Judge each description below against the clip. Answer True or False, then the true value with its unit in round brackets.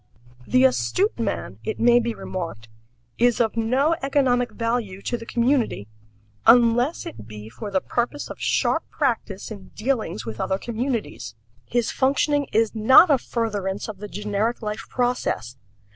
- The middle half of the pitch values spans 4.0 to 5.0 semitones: True (4.3 semitones)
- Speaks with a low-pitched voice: False (230 Hz)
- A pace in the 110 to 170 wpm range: True (150 wpm)